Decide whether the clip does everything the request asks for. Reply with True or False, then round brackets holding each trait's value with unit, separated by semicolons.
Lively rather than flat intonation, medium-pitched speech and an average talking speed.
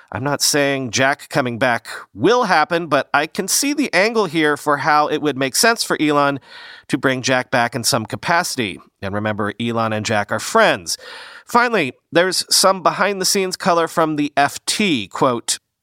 True (6.4 semitones; 150 Hz; 180 wpm)